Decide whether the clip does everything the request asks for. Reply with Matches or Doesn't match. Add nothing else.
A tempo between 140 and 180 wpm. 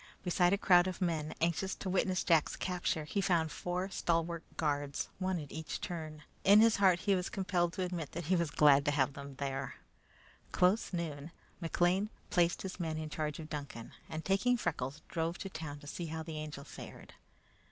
Doesn't match